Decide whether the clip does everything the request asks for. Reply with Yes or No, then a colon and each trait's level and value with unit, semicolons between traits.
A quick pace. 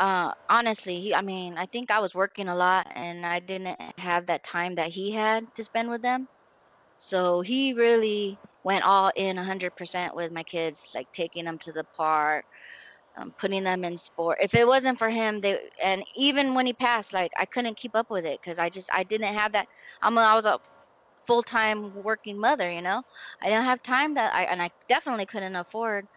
Yes: fast, 210 wpm